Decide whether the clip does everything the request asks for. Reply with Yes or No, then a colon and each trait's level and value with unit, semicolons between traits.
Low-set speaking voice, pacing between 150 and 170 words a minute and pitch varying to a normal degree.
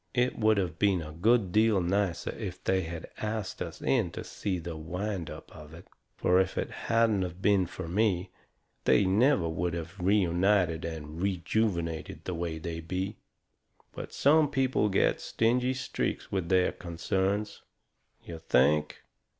Yes: very low, 95 Hz; average, 160 wpm; average, 4.0 semitones